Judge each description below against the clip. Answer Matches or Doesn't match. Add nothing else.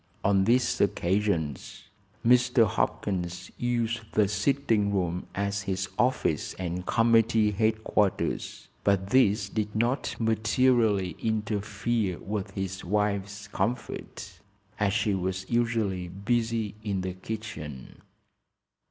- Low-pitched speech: Matches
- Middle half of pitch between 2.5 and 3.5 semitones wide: Matches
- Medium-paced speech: Doesn't match